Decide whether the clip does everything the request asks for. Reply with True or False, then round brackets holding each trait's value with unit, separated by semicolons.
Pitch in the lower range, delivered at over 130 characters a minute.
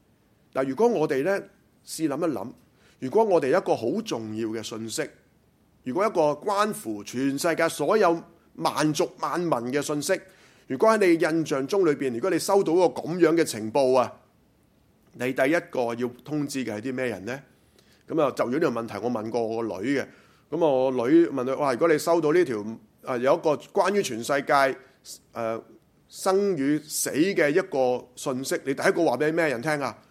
False (145 Hz; 260 characters per minute)